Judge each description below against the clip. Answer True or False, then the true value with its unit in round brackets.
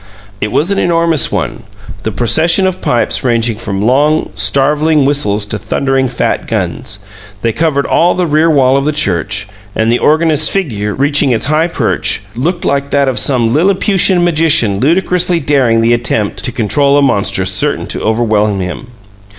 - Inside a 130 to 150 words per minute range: False (165 wpm)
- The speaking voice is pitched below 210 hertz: True (140 Hz)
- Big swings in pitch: True (5.7 semitones)